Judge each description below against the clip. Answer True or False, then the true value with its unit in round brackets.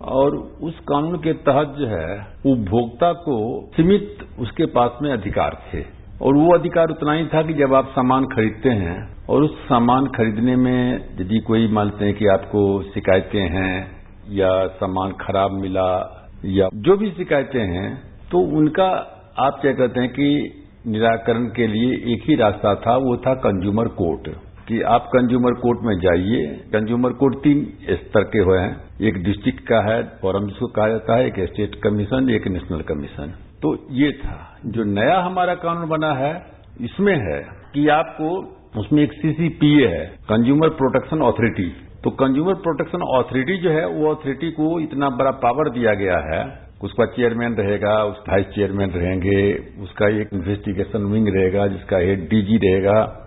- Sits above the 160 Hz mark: False (115 Hz)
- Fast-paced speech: False (165 wpm)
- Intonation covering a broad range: True (6.0 semitones)